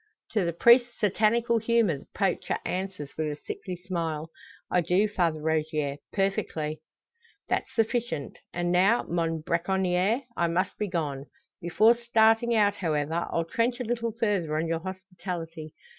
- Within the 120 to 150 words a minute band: Yes, average, 145 wpm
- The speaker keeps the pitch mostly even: No, average, 5.2 semitones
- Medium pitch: Yes, medium, 180 Hz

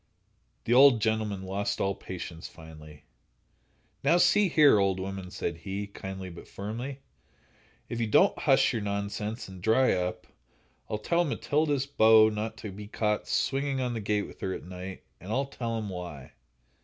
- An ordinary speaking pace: Yes, average, 170 wpm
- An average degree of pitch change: Yes, average, 3.9 semitones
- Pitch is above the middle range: No, low, 105 Hz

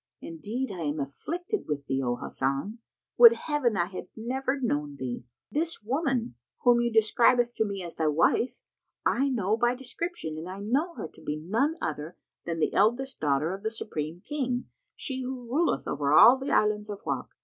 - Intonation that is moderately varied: No, wide, 8.6 semitones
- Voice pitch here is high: Yes, high, 220 Hz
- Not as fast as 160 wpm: No, average, 185 wpm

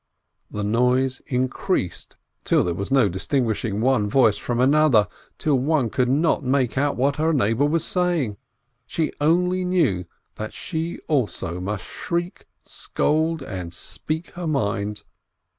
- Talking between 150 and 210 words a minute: No, average, 140 wpm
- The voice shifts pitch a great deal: Yes, wide, 6.9 semitones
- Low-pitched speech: Yes, low, 130 Hz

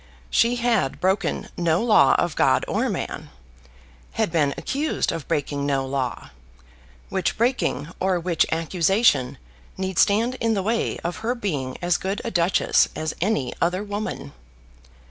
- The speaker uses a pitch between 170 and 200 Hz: Yes, medium, 185 Hz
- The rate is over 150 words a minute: No, average, 145 wpm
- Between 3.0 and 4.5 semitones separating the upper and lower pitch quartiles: No, wide, 5.6 semitones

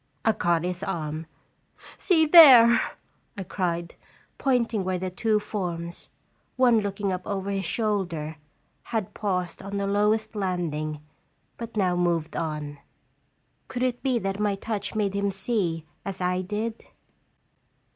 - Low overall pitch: No, high, 195 Hz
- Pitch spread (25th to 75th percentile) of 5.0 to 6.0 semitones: No, average, 3.8 semitones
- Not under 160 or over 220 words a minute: No, slow, 135 wpm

